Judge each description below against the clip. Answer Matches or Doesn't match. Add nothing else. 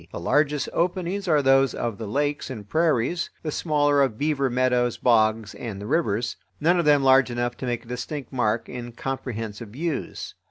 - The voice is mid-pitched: Doesn't match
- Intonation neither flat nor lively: Matches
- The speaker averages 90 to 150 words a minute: Doesn't match